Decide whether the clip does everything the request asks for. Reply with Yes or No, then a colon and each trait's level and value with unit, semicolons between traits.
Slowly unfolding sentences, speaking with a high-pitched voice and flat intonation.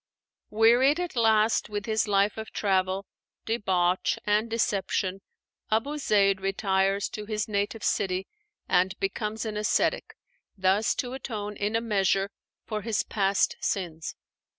Yes: slow, 130 wpm; high, 210 Hz; narrow, 2.2 semitones